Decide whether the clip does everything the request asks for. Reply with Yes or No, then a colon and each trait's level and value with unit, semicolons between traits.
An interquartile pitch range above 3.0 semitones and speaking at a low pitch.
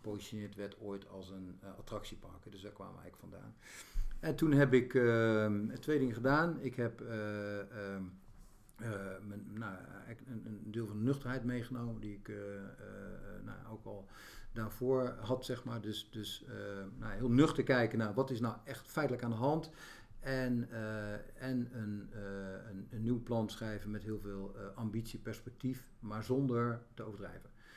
Yes: average, 3.5 semitones; low, 110 Hz